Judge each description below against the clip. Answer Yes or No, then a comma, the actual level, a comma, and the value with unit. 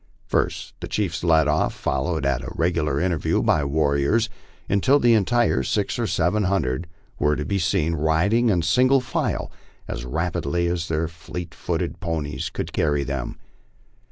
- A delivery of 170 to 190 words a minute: No, average, 155 wpm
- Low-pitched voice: Yes, very low, 80 Hz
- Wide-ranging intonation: No, average, 3.9 semitones